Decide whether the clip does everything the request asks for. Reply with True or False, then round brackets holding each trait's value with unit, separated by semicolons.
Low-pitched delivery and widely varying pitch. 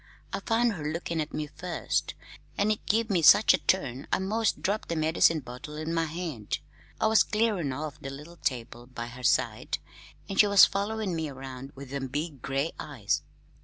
False (155 Hz; 6.4 semitones)